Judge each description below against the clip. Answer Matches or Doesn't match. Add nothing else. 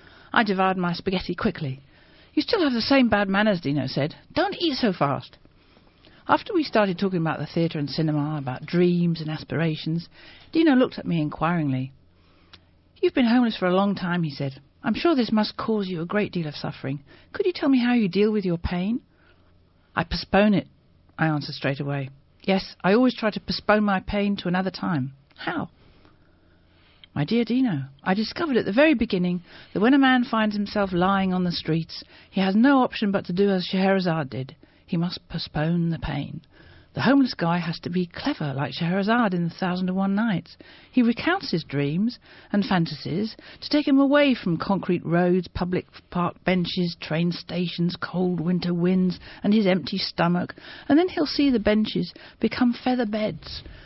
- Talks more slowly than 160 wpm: Doesn't match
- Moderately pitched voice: Matches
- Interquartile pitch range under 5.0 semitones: Doesn't match